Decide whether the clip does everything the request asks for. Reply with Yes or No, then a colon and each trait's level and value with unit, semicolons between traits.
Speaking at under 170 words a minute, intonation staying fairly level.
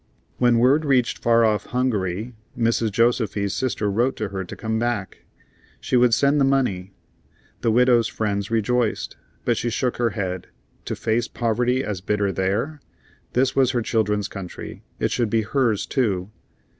No: average, 160 wpm; average, 3.2 semitones